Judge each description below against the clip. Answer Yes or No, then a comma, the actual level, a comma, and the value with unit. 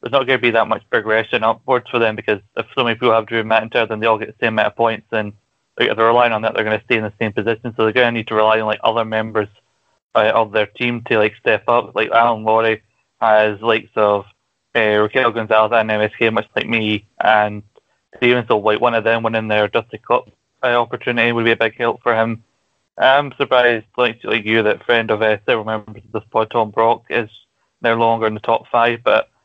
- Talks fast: Yes, fast, 250 wpm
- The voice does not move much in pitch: Yes, narrow, 1.4 semitones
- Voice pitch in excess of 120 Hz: No, low, 115 Hz